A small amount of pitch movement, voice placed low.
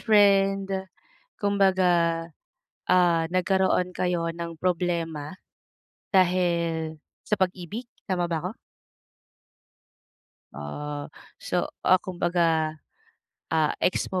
No: narrow, 2.1 semitones; medium, 175 Hz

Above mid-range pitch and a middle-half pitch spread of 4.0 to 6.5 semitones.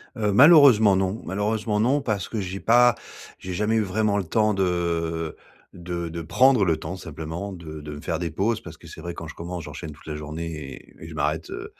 No: very low, 95 Hz; average, 4.5 semitones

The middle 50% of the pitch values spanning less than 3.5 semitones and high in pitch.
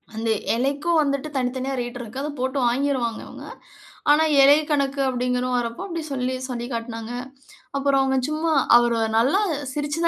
Yes: average, 2.9 semitones; very high, 260 Hz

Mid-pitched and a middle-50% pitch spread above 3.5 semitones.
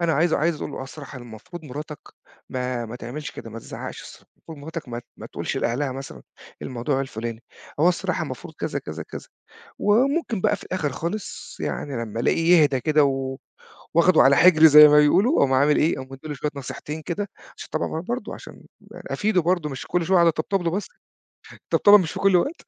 Yes: medium, 150 Hz; average, 4.6 semitones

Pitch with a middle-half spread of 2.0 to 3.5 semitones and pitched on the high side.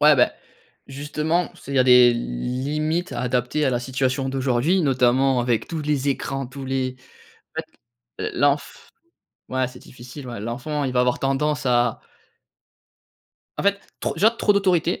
No: average, 3.2 semitones; low, 135 Hz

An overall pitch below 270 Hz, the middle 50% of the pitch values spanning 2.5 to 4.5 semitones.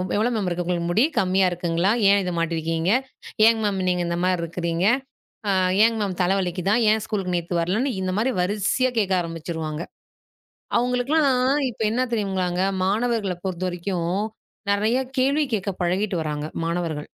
Yes: medium, 185 Hz; average, 3.8 semitones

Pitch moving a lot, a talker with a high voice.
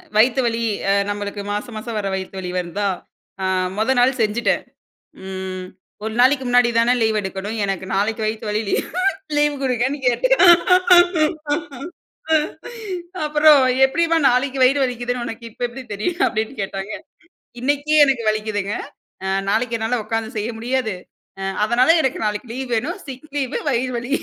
No: average, 3.8 semitones; high, 235 Hz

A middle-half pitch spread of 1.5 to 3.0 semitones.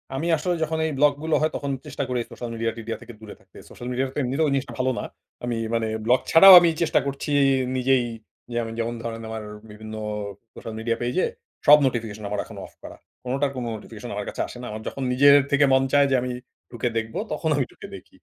No: average, 3.7 semitones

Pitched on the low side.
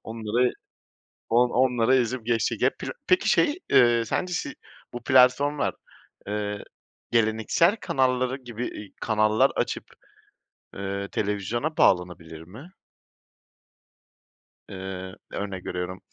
Yes: low, 115 Hz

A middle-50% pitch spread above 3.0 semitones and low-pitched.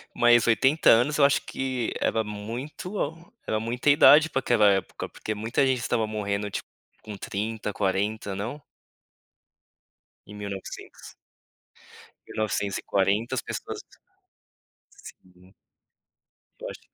Yes: average, 4.0 semitones; low, 110 Hz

